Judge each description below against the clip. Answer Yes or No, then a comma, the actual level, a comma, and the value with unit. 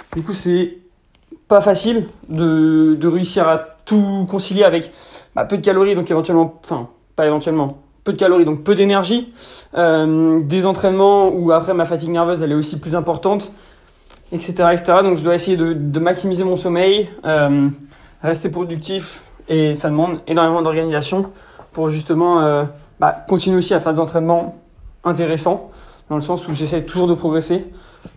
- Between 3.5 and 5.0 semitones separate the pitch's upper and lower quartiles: No, average, 2.8 semitones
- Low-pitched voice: No, medium, 170 Hz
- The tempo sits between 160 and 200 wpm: Yes, average, 165 wpm